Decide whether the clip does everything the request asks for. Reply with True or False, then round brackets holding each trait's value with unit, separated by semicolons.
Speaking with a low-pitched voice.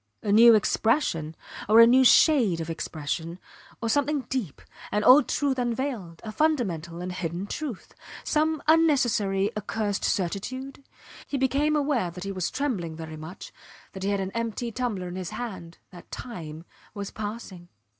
False (210 Hz)